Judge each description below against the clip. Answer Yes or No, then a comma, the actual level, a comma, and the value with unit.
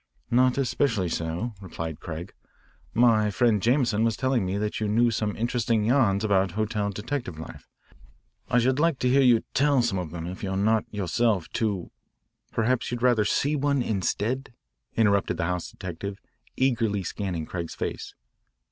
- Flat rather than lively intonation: No, average, 4.3 semitones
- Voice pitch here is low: Yes, low, 110 Hz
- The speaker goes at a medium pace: Yes, average, 165 wpm